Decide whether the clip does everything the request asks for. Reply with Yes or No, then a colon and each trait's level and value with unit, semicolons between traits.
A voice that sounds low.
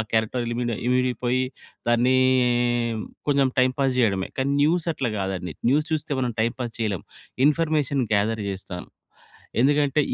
Yes: low, 125 Hz